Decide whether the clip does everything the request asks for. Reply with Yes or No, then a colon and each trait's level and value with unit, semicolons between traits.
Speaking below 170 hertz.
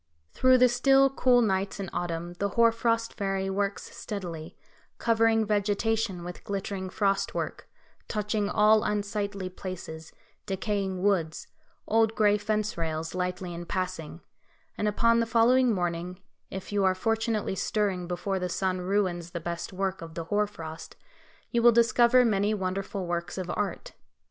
No: high, 200 Hz